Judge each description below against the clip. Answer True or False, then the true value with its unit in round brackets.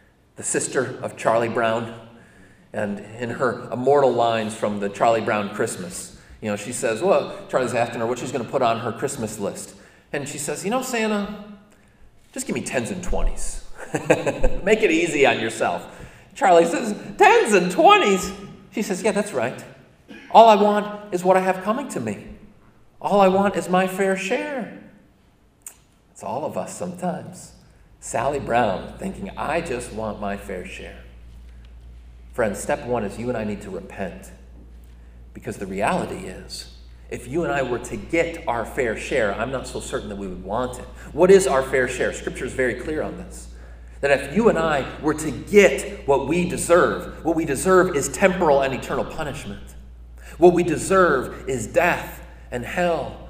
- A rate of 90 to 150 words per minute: False (180 wpm)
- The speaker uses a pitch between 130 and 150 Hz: True (135 Hz)